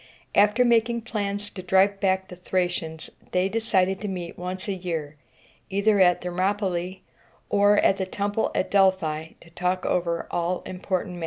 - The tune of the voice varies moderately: No, narrow, 2.2 semitones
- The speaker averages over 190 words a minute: No, average, 160 wpm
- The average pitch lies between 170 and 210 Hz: Yes, high, 190 Hz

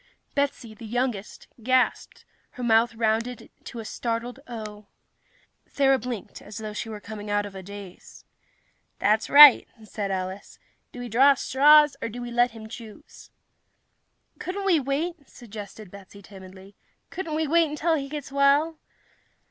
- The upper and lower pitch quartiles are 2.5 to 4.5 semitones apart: No, average, 5.0 semitones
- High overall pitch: Yes, high, 235 Hz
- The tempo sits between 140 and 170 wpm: Yes, average, 155 wpm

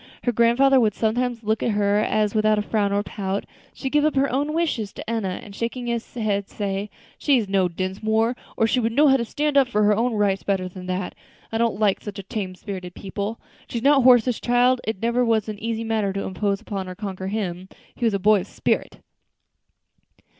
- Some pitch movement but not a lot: Yes, average, 3.2 semitones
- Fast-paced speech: Yes, fast, 220 wpm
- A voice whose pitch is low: No, high, 215 Hz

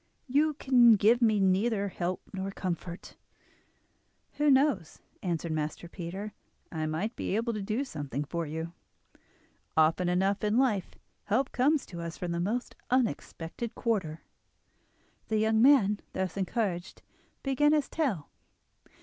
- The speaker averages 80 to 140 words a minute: Yes, slow, 135 wpm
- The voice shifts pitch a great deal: Yes, wide, 5.8 semitones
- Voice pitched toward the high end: Yes, high, 200 Hz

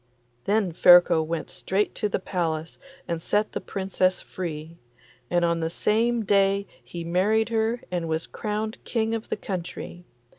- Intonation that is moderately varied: Yes, average, 4.0 semitones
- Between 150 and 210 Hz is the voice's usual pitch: Yes, medium, 185 Hz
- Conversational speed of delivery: Yes, average, 155 wpm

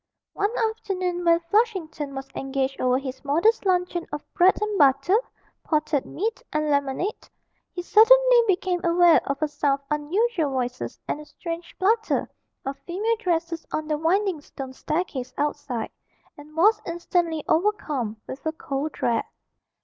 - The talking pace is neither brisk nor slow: Yes, average, 150 wpm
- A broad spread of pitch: No, average, 4.9 semitones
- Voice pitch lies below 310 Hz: No, very high, 325 Hz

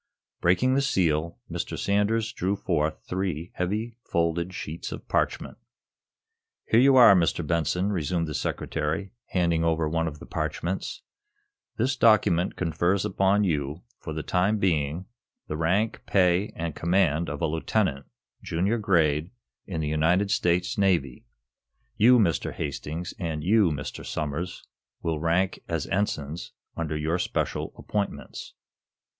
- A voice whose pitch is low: Yes, very low, 85 Hz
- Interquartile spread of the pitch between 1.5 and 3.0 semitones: No, average, 3.7 semitones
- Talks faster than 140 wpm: No, slow, 135 wpm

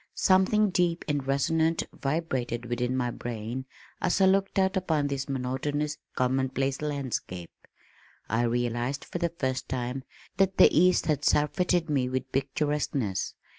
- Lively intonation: No, average, 4.7 semitones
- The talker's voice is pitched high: No, medium, 140 Hz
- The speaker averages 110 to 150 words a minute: Yes, slow, 135 wpm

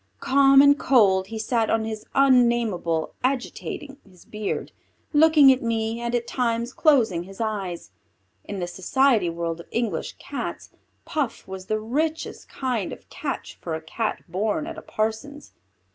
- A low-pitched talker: No, high, 225 Hz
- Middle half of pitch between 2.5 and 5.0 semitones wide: No, wide, 5.6 semitones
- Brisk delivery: No, average, 155 wpm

